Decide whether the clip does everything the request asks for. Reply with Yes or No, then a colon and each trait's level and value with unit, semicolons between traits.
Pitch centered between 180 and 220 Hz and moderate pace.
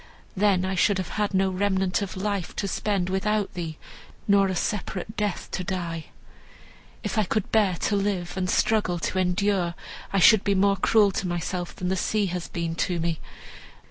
Yes: high, 190 Hz; average, 185 wpm